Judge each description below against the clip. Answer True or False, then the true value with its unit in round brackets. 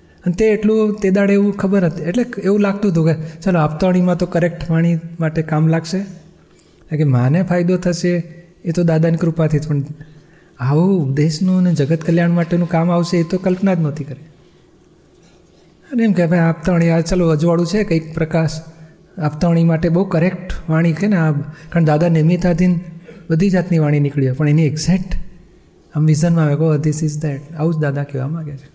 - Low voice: False (170 Hz)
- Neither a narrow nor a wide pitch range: False (2.1 semitones)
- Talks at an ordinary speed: False (185 wpm)